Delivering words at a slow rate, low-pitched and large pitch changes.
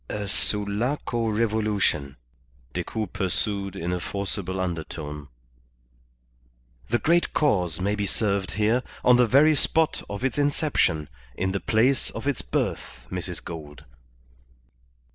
No: slow, 125 wpm; low, 105 Hz; average, 4.5 semitones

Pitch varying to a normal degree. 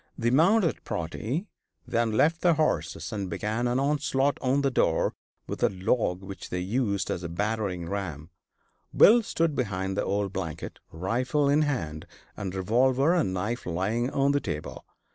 No: wide, 6.8 semitones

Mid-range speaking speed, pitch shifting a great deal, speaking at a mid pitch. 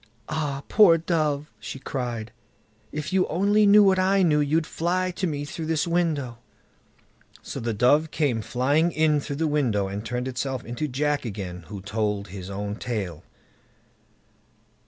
Yes: average, 155 wpm; wide, 6.0 semitones; medium, 145 Hz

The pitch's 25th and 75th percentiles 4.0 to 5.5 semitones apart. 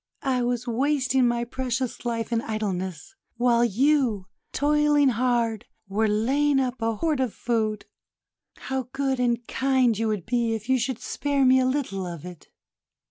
No: average, 2.9 semitones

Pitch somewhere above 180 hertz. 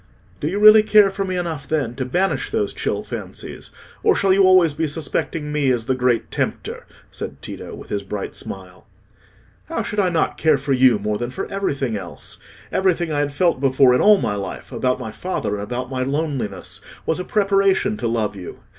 No: medium, 140 Hz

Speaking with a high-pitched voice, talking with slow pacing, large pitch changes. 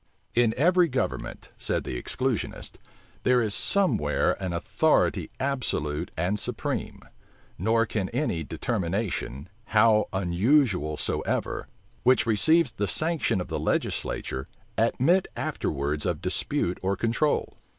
No: low, 110 Hz; slow, 120 wpm; wide, 6.9 semitones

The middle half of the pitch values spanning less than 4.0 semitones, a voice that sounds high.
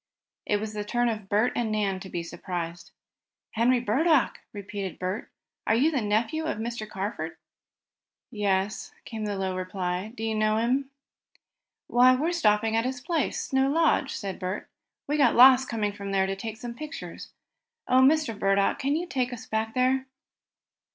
No: average, 4.4 semitones; high, 220 Hz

